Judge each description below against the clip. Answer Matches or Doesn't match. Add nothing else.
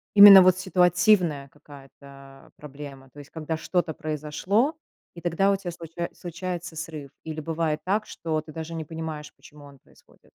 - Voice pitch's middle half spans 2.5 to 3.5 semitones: Matches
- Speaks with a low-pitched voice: Doesn't match